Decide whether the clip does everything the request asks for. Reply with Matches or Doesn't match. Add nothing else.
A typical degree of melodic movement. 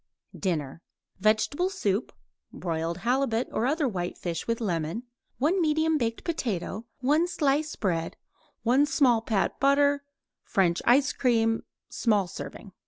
Doesn't match